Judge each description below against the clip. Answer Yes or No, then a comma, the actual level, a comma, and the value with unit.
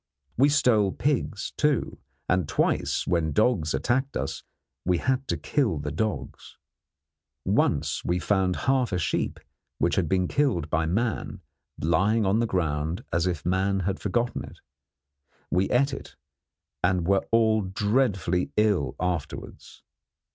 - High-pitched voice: No, very low, 95 Hz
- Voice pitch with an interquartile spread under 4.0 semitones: No, average, 5.2 semitones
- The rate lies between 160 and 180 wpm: No, average, 140 wpm